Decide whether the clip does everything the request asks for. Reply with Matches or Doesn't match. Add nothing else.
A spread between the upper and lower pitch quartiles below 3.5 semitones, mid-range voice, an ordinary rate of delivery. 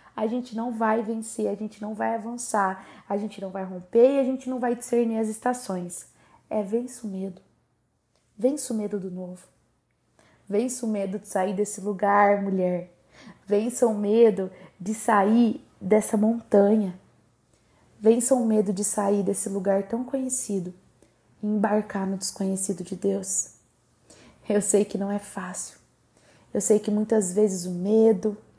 Doesn't match